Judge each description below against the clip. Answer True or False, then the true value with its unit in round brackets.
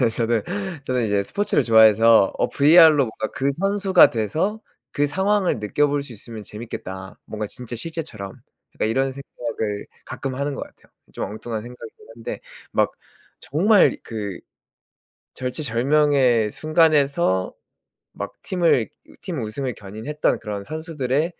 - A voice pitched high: False (125 Hz)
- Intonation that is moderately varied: False (5.8 semitones)